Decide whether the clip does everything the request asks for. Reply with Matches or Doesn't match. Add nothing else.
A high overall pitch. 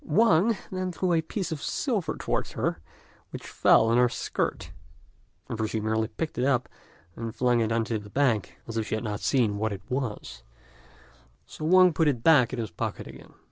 Doesn't match